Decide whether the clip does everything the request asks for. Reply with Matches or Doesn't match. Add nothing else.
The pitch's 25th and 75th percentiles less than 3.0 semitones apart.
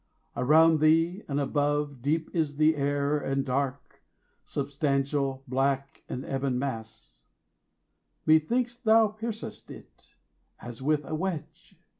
Matches